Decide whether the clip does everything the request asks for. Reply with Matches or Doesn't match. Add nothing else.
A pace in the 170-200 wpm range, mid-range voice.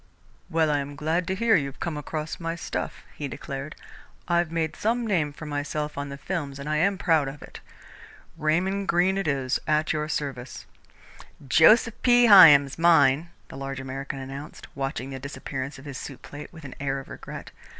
Matches